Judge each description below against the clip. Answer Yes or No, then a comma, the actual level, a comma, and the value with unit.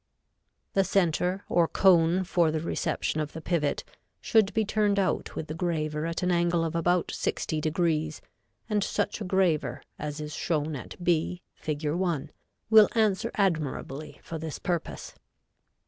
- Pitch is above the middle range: No, medium, 170 Hz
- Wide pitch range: No, average, 3.3 semitones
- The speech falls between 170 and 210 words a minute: No, average, 150 wpm